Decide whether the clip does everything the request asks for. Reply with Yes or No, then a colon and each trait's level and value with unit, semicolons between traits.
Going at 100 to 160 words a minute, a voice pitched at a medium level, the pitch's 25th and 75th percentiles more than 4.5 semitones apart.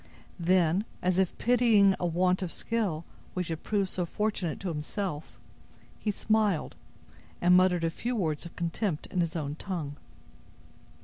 No: average, 150 wpm; medium, 180 Hz; average, 3.3 semitones